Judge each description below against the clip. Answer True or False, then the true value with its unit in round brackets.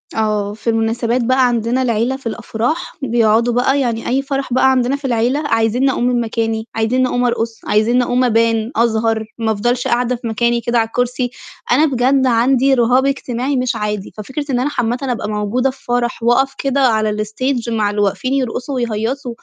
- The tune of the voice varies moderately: False (2.3 semitones)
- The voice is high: True (240 Hz)